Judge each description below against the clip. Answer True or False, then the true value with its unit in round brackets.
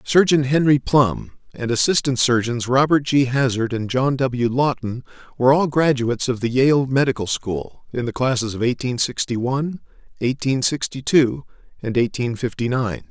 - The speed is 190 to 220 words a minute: False (160 wpm)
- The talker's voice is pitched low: True (125 Hz)